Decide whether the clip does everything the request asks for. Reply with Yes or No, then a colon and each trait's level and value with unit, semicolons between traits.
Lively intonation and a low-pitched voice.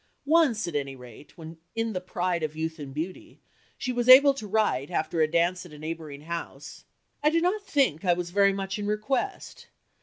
No: wide, 6.3 semitones; medium, 180 Hz